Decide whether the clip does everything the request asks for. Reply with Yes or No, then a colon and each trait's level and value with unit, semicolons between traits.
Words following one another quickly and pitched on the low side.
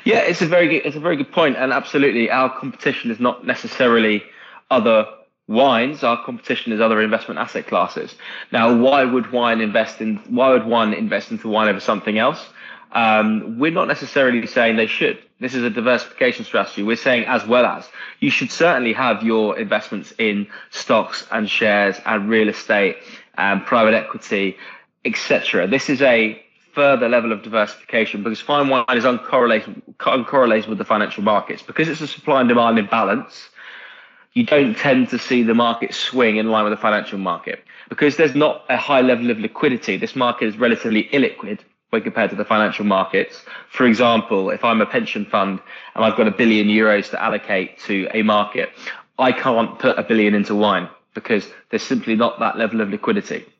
Yes: fast, 185 wpm; low, 115 Hz